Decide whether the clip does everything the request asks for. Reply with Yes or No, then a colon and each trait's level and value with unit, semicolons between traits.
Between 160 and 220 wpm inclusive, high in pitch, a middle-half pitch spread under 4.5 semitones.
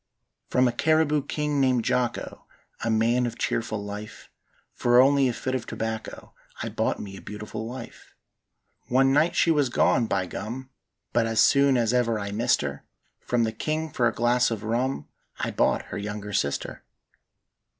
No: average, 170 wpm; low, 120 Hz; average, 3.2 semitones